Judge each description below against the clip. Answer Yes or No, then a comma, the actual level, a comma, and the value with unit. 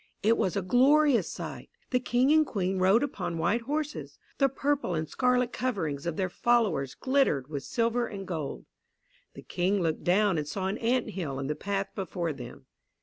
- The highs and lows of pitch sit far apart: Yes, wide, 6.8 semitones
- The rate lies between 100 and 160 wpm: No, average, 185 wpm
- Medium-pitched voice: No, high, 195 Hz